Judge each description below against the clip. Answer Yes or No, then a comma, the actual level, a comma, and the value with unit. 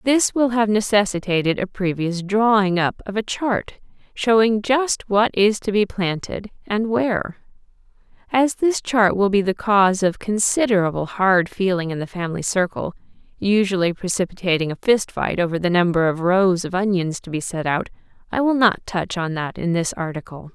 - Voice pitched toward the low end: No, high, 195 Hz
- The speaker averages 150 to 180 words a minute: Yes, average, 175 wpm